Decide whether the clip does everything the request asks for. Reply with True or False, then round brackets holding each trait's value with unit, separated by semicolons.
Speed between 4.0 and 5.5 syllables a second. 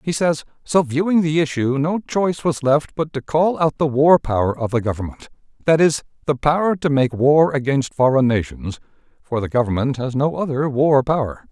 True (5.2 syllables/s)